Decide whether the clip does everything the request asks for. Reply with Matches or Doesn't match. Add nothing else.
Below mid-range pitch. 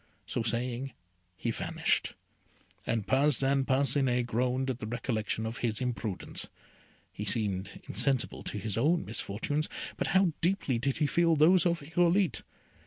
Matches